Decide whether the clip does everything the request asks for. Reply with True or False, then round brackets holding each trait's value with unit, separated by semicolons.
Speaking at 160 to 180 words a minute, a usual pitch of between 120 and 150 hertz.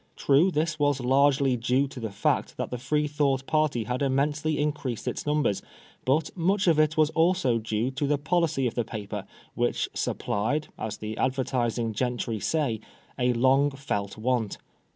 True (165 wpm; 135 Hz)